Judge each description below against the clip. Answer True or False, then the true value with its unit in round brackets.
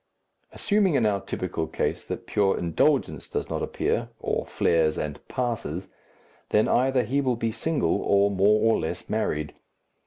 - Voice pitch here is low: True (105 Hz)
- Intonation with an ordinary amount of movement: False (6.0 semitones)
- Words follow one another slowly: False (155 wpm)